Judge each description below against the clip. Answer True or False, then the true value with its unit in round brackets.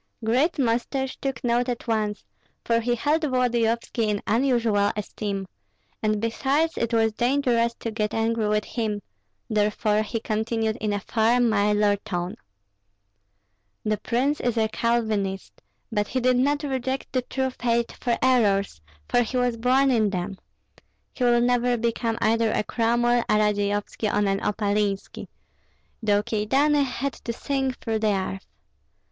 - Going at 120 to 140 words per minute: False (150 wpm)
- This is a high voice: True (230 Hz)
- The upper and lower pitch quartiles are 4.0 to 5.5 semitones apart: False (2.7 semitones)